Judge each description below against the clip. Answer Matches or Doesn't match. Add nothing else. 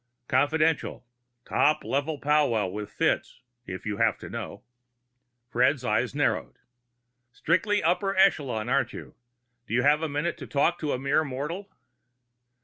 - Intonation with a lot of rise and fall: Doesn't match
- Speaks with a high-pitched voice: Doesn't match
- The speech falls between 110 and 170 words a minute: Matches